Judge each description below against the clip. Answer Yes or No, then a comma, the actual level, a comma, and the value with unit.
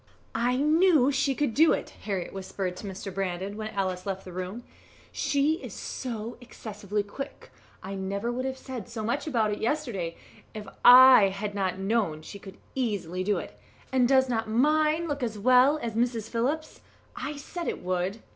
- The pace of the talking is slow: No, average, 180 wpm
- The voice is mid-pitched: No, high, 225 Hz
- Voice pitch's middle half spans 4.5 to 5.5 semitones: Yes, average, 5.1 semitones